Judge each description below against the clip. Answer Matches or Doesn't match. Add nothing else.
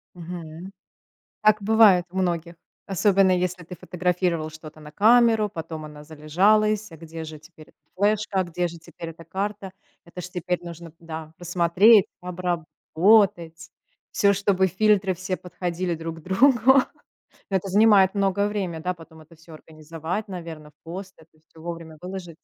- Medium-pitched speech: Matches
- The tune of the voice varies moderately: Matches